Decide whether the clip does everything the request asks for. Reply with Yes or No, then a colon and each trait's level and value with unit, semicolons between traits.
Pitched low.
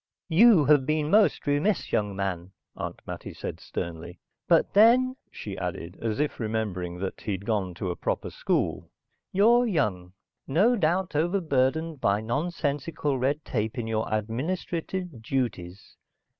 Yes: low, 130 Hz